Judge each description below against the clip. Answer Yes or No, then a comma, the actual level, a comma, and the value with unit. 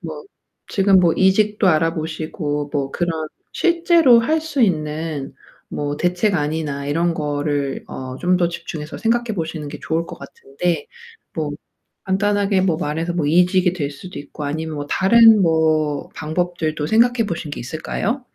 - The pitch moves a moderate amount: Yes, average, 4.3 semitones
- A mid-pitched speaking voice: Yes, medium, 165 Hz